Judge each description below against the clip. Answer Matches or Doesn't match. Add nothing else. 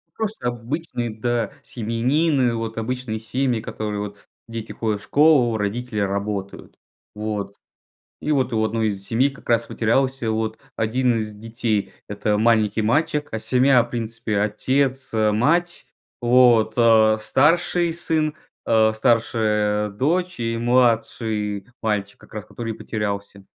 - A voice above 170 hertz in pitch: Doesn't match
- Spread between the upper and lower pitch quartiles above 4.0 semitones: Doesn't match